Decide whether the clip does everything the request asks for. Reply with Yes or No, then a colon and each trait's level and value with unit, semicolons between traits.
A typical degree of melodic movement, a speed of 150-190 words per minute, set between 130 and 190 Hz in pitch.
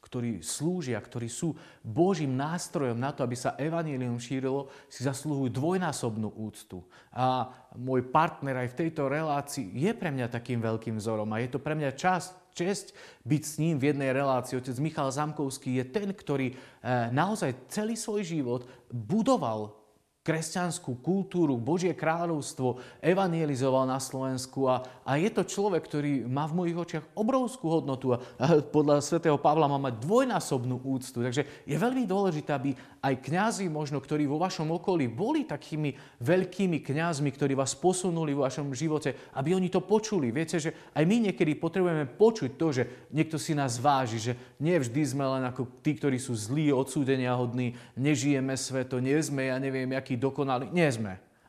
Yes: average, 4.4 semitones; fast, 165 wpm; medium, 140 Hz